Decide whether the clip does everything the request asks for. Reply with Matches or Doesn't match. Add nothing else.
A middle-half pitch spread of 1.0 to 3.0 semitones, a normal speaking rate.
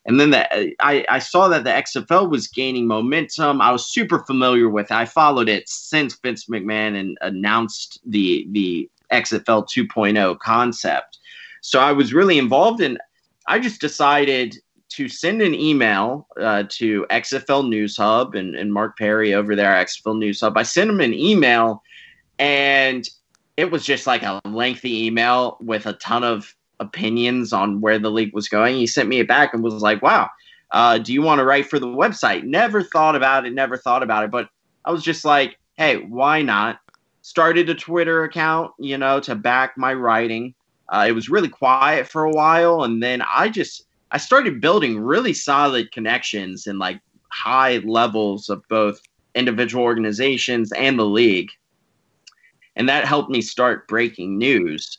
Doesn't match